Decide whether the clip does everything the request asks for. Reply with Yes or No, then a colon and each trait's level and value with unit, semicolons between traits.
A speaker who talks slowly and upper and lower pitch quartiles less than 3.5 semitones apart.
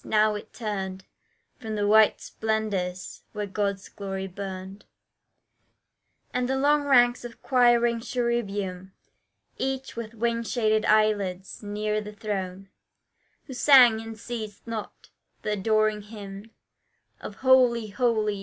Yes: slow, 120 wpm; average, 2.8 semitones